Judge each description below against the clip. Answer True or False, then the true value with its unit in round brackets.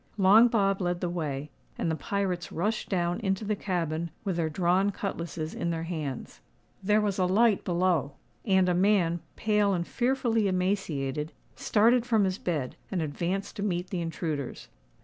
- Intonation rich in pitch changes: False (3.3 semitones)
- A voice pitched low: False (185 Hz)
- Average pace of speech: True (170 wpm)